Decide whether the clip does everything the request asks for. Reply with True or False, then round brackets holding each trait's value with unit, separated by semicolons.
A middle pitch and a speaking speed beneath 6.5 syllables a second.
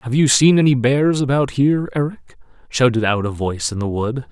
False (125 Hz; 5.5 syllables/s)